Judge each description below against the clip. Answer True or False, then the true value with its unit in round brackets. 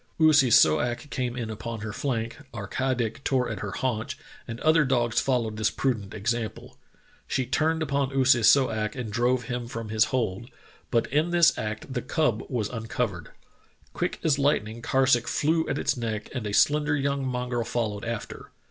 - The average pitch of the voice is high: False (120 Hz)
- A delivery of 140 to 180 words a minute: False (190 wpm)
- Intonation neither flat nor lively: True (3.4 semitones)